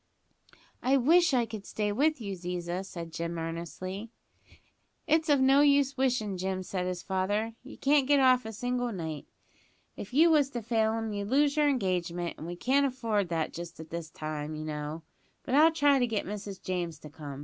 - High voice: Yes, high, 210 Hz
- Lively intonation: Yes, wide, 7.4 semitones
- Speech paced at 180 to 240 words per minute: Yes, average, 195 wpm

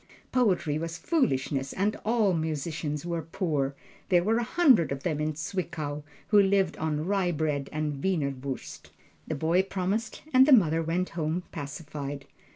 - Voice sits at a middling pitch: Yes, medium, 165 Hz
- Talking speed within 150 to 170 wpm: Yes, average, 155 wpm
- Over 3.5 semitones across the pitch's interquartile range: Yes, average, 4.4 semitones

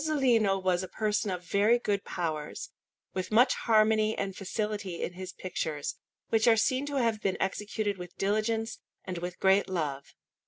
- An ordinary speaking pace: Yes, average, 170 wpm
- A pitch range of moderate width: Yes, average, 3.3 semitones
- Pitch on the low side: No, high, 200 Hz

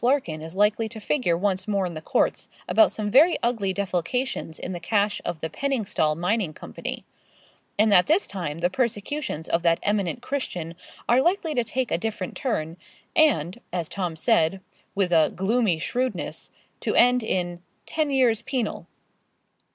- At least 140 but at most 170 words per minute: Yes, average, 165 wpm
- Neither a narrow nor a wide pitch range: No, wide, 6.2 semitones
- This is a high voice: Yes, high, 200 Hz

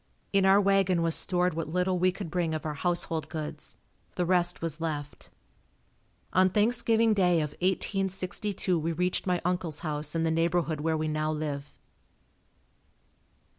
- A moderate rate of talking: Yes, average, 155 wpm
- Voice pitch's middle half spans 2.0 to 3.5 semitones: Yes, average, 2.9 semitones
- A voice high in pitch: No, medium, 175 Hz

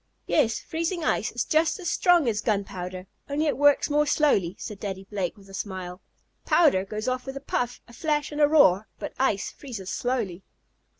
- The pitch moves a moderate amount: No, wide, 7.2 semitones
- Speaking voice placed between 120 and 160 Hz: No, high, 245 Hz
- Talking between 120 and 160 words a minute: No, average, 190 wpm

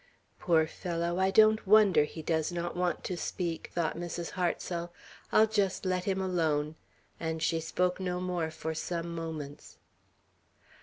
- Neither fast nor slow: Yes, average, 150 wpm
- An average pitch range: No, narrow, 2.2 semitones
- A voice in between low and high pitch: Yes, medium, 175 Hz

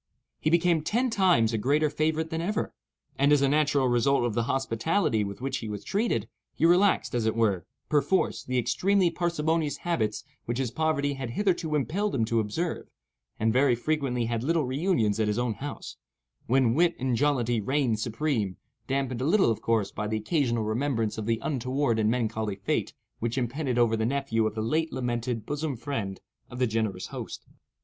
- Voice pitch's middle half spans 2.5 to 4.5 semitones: No, average, 5.3 semitones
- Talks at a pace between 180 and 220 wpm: Yes, average, 185 wpm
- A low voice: Yes, low, 130 Hz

